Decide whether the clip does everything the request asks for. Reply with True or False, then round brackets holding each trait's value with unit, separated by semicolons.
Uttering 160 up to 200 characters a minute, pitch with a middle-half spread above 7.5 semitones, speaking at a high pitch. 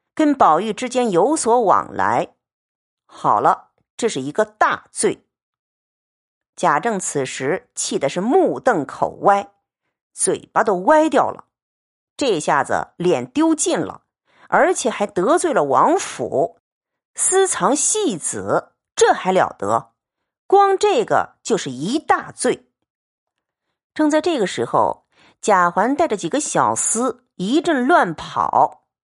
True (170 characters per minute; 8.8 semitones; 265 Hz)